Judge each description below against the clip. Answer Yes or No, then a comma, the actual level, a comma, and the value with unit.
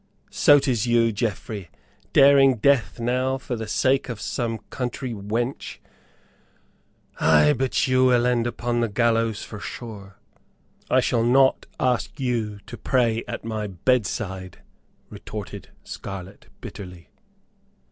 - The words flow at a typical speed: No, slow, 125 wpm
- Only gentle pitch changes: No, average, 3.5 semitones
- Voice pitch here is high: No, low, 115 Hz